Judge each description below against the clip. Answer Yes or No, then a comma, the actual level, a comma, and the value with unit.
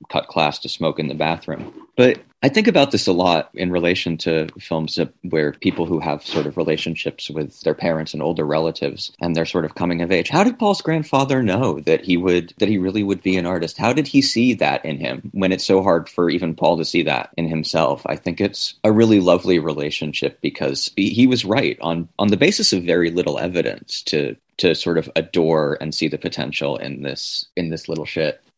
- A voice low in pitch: Yes, very low, 85 Hz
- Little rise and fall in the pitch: No, average, 3.9 semitones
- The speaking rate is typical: No, fast, 225 wpm